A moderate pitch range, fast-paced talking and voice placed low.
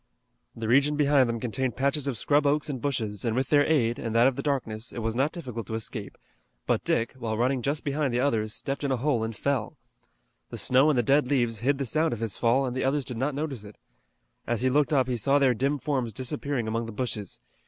Yes: average, 3.5 semitones; fast, 245 wpm; low, 130 Hz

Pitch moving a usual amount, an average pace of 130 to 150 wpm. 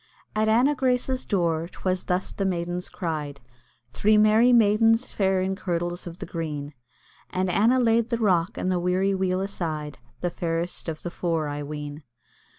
No: average, 4.3 semitones; average, 165 wpm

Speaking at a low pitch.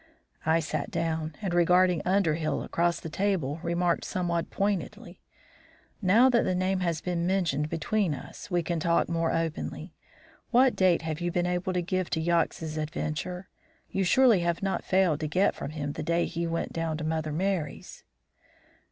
No: medium, 170 Hz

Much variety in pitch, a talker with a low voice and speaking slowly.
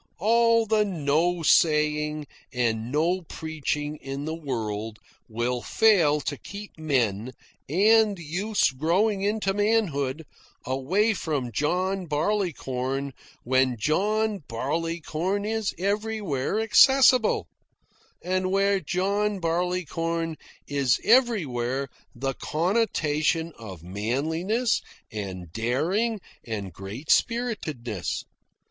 No: wide, 7.2 semitones; medium, 160 Hz; slow, 95 wpm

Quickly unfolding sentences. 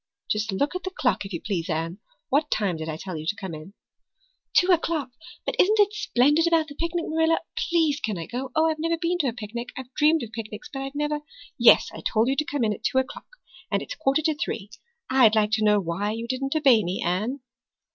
Yes: fast, 240 wpm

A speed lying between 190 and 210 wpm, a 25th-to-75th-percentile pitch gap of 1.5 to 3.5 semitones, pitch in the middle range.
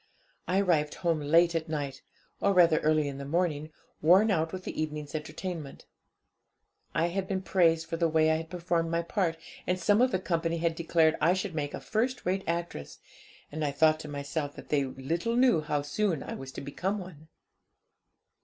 Yes: average, 200 wpm; average, 3.2 semitones; medium, 165 Hz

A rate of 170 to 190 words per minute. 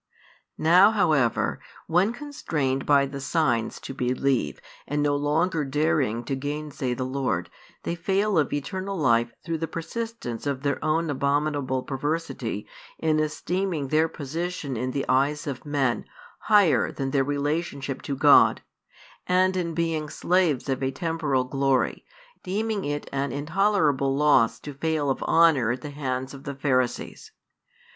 No: average, 145 wpm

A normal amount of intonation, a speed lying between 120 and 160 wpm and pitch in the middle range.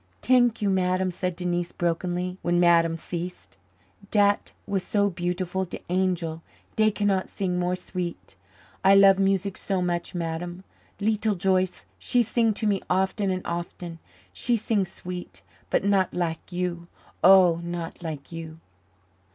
No: narrow, 2.1 semitones; average, 145 wpm; medium, 180 Hz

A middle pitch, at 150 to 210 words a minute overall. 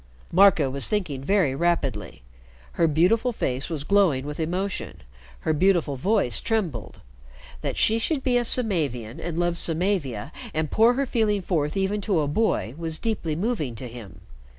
Yes: medium, 170 Hz; average, 160 wpm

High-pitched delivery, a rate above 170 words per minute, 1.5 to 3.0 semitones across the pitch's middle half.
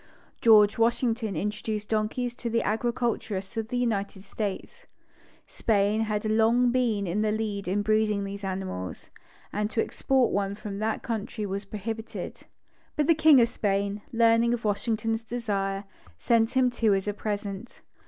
No: high, 215 Hz; average, 155 wpm; narrow, 2.4 semitones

